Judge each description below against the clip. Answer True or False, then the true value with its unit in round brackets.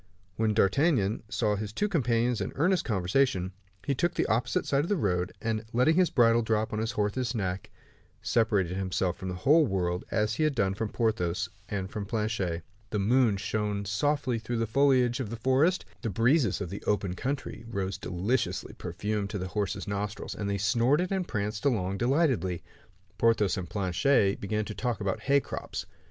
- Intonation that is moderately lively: True (4.5 semitones)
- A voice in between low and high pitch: False (110 Hz)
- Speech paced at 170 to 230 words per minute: True (185 wpm)